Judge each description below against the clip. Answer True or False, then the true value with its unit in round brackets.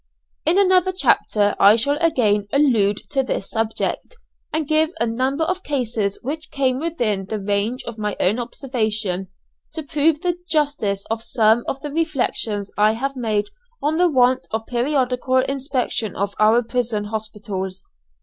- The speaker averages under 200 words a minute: True (155 wpm)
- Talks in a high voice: True (245 Hz)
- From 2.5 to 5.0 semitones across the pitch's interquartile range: False (5.4 semitones)